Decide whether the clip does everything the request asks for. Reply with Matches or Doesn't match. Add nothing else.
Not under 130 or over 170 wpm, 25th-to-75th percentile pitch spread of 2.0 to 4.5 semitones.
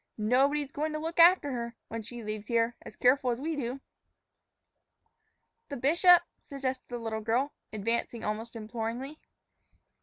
Matches